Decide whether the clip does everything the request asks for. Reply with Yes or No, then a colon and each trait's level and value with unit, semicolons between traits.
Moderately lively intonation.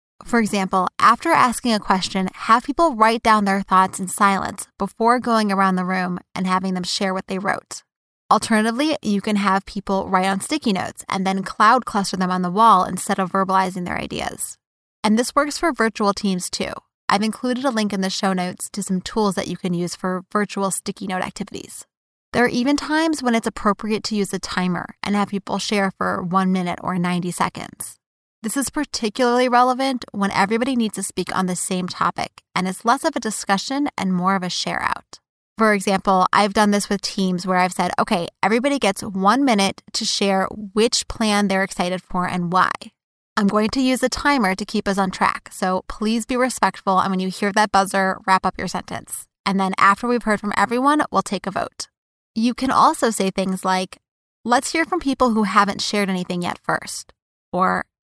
Yes: average, 3.3 semitones